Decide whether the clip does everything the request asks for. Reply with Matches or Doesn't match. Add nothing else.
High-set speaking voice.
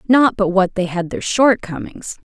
Matches